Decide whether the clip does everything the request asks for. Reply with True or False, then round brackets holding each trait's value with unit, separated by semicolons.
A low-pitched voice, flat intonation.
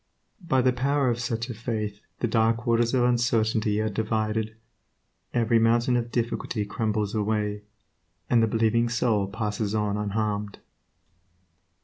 True (110 Hz; 1.9 semitones)